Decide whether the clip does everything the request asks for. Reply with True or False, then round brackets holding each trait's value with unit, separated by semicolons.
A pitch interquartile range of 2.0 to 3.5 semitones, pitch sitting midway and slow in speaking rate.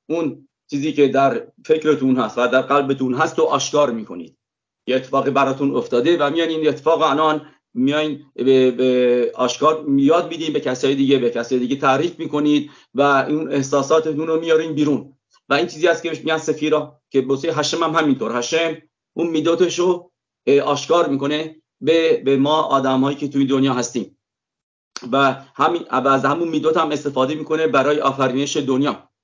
False (2.7 semitones; 145 Hz; 160 wpm)